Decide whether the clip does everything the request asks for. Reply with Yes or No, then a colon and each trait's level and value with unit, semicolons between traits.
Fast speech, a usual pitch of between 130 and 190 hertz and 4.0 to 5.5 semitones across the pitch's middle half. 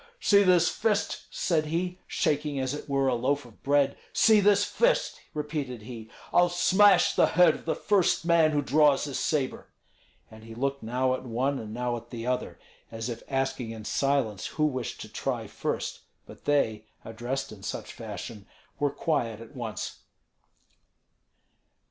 No: average, 165 wpm; low, 135 Hz; average, 4.7 semitones